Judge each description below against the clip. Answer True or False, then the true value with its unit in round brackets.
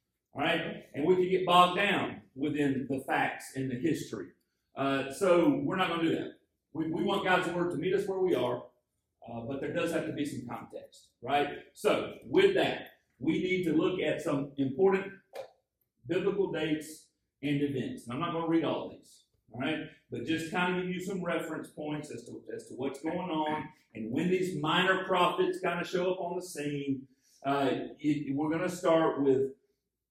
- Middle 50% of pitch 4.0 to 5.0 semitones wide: True (4.5 semitones)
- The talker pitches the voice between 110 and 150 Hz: False (160 Hz)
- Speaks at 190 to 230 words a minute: True (200 wpm)